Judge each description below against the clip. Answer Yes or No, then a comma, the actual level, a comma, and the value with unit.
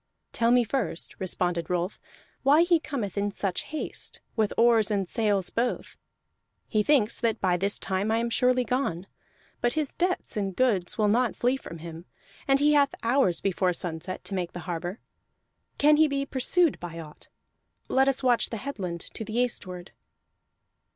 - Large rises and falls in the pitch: Yes, wide, 6.1 semitones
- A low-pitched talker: No, high, 220 Hz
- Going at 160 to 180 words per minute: Yes, average, 170 wpm